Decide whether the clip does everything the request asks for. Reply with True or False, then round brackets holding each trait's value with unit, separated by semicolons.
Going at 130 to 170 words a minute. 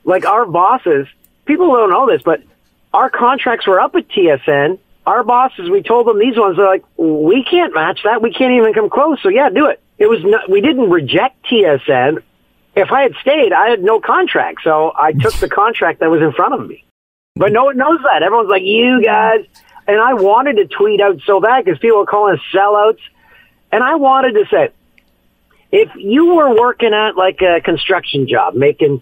False (205 wpm)